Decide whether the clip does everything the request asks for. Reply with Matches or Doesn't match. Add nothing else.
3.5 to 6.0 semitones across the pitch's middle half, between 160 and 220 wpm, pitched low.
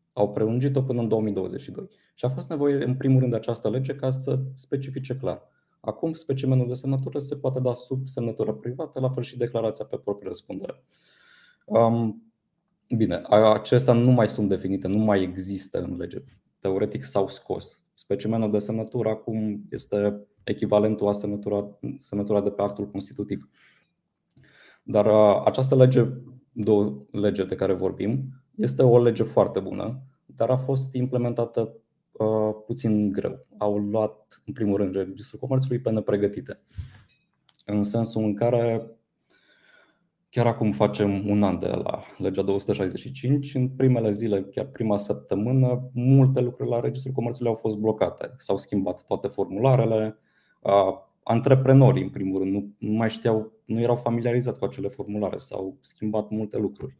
Doesn't match